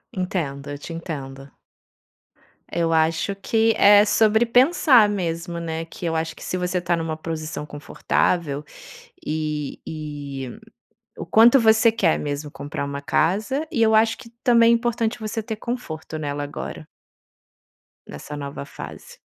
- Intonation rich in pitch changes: Yes, wide, 6.7 semitones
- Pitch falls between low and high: Yes, medium, 165 Hz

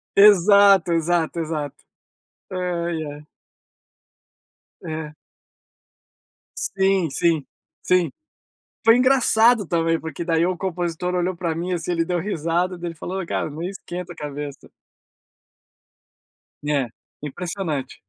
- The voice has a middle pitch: Yes, medium, 170 Hz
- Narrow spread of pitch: Yes, narrow, 2.3 semitones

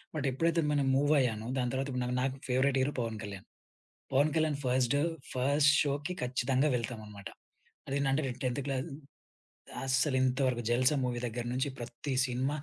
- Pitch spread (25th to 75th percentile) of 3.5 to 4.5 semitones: No, narrow, 2.4 semitones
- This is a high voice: No, low, 130 Hz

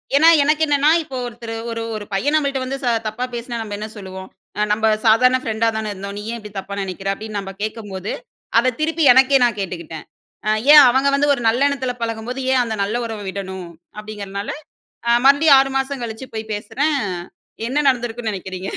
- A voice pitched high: Yes, high, 230 Hz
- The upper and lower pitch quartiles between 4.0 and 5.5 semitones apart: Yes, average, 4.7 semitones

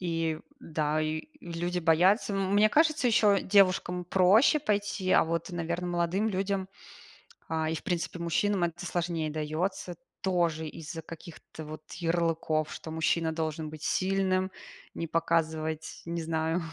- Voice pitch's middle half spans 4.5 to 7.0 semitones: No, average, 2.8 semitones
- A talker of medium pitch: Yes, medium, 170 Hz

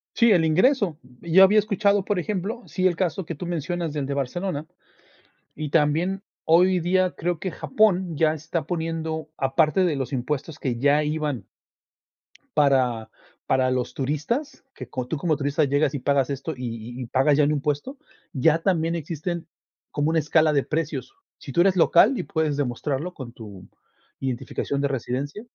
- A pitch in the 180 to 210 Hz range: No, medium, 155 Hz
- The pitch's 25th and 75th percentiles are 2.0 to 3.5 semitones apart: No, average, 4.1 semitones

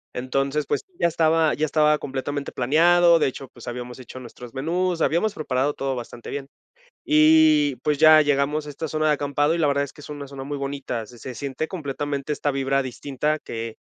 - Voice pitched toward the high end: No, medium, 145 Hz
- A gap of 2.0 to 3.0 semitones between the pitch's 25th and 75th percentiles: Yes, average, 2.7 semitones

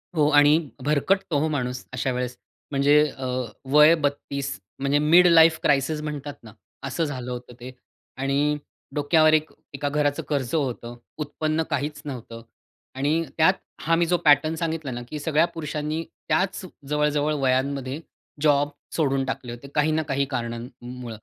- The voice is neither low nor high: Yes, medium, 145 Hz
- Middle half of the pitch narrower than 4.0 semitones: Yes, average, 2.7 semitones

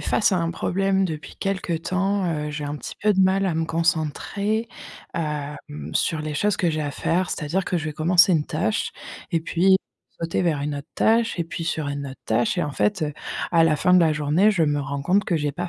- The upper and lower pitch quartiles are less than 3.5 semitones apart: No, average, 4.0 semitones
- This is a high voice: No, medium, 165 Hz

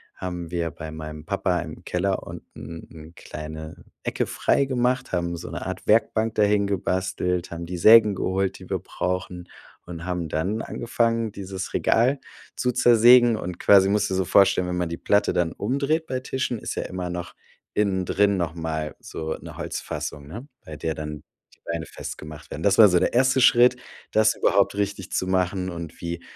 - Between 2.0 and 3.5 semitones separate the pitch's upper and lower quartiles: No, average, 4.3 semitones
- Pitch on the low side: Yes, very low, 95 Hz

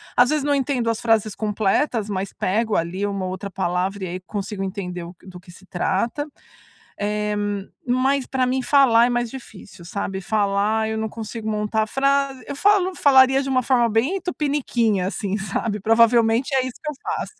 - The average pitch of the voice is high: Yes, high, 220 Hz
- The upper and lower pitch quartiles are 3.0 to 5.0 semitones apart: Yes, average, 4.6 semitones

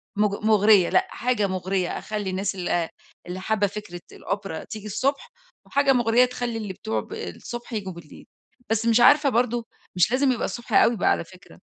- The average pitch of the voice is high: Yes, high, 210 Hz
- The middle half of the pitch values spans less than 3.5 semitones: No, average, 4.3 semitones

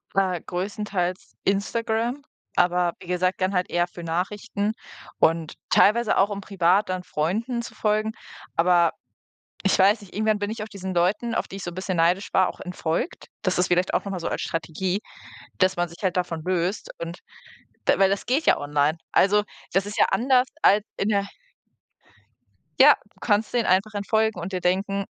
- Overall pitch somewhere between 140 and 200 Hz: Yes, high, 190 Hz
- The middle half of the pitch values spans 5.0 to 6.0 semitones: No, average, 2.8 semitones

